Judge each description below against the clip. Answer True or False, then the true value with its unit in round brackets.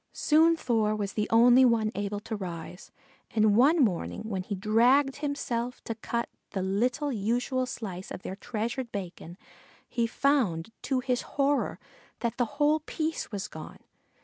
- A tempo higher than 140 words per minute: True (155 wpm)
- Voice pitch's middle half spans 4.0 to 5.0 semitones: True (4.3 semitones)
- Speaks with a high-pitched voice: True (230 Hz)